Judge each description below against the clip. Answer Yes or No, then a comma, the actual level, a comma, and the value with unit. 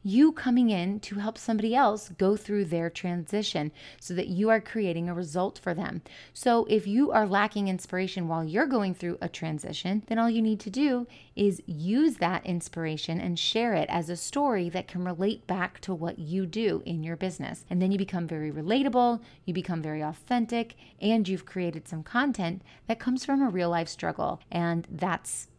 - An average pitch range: Yes, average, 4.5 semitones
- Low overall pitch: No, high, 190 Hz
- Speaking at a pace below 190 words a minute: No, average, 195 wpm